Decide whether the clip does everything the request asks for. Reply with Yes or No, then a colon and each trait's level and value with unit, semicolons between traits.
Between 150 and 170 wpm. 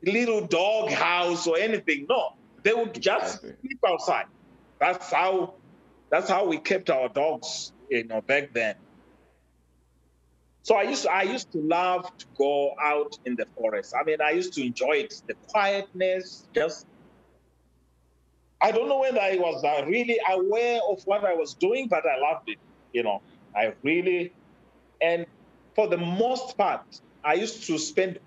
Yes: average, 165 wpm